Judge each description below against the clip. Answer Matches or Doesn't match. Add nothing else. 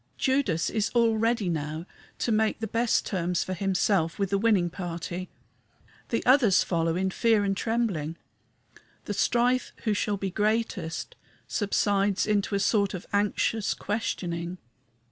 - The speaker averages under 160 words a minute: Matches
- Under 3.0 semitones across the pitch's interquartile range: Doesn't match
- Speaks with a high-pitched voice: Matches